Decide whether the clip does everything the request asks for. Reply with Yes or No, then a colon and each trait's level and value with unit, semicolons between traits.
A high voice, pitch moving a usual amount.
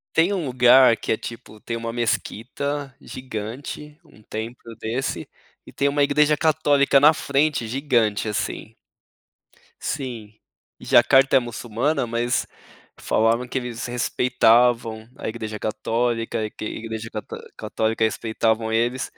No: low, 120 Hz; average, 3.4 semitones